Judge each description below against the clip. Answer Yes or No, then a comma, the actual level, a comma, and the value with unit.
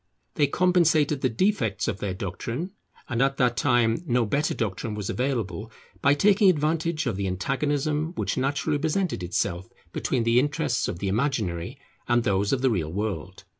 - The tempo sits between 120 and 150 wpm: No, average, 170 wpm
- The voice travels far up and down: Yes, wide, 6.6 semitones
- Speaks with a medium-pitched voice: No, low, 125 Hz